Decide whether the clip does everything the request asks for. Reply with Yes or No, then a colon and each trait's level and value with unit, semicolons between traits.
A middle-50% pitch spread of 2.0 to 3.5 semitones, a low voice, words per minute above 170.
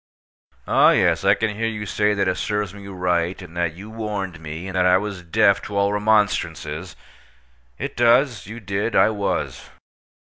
Yes: average, 2.8 semitones; low, 100 Hz; average, 180 wpm